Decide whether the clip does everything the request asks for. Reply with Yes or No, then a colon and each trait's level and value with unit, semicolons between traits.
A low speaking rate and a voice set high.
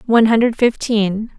Yes: slow, 130 wpm; high, 220 Hz